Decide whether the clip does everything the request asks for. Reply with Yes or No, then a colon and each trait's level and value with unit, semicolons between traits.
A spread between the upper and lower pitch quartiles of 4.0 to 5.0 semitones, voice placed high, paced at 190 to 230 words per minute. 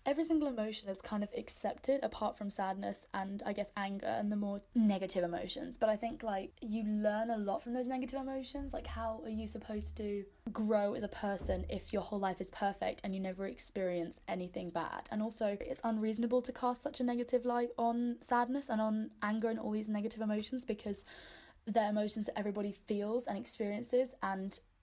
No: average, 3.1 semitones; high, 215 Hz; average, 200 wpm